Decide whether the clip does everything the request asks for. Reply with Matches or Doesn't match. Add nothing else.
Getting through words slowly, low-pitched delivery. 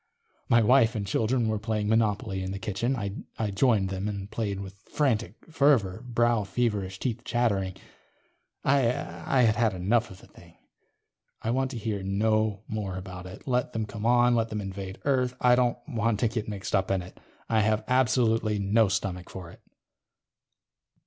Doesn't match